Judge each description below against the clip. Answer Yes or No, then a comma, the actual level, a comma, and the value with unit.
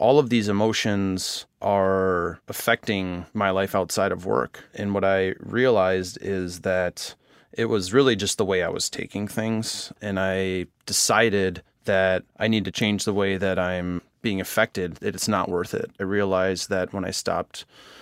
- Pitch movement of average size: No, narrow, 1.6 semitones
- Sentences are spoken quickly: No, average, 170 wpm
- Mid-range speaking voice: No, very low, 95 Hz